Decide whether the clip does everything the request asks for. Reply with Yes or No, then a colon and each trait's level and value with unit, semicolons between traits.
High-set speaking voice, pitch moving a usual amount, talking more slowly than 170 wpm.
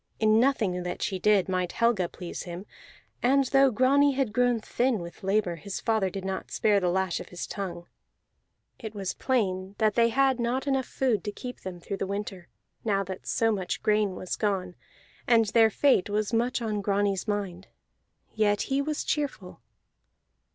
No: high, 210 Hz; average, 4.2 semitones; average, 180 wpm